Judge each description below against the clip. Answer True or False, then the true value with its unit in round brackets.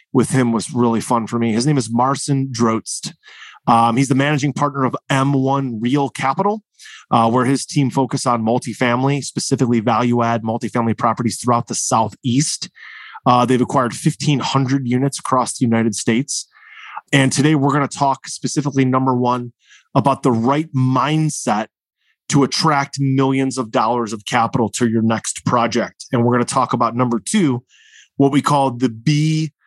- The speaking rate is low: False (165 wpm)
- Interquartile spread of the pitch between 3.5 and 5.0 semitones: False (2.7 semitones)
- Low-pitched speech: True (130 Hz)